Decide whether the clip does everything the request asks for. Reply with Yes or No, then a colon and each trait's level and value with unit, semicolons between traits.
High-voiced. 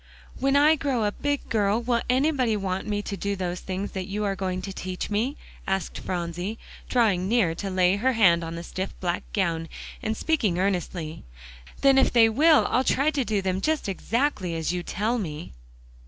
Yes: high, 200 Hz